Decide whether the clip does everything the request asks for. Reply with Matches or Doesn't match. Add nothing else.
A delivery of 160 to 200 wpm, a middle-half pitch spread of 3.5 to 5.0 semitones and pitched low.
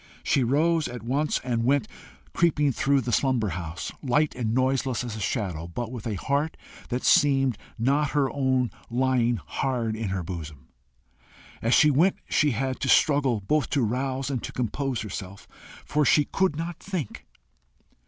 Matches